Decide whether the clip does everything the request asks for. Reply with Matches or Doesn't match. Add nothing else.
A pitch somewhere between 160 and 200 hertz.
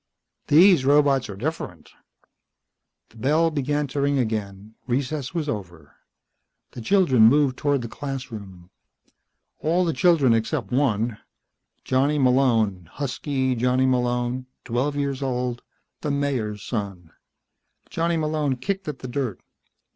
Doesn't match